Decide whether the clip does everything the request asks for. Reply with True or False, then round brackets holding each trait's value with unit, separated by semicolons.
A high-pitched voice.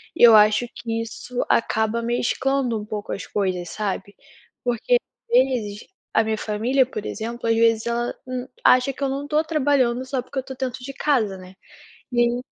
True (240 Hz)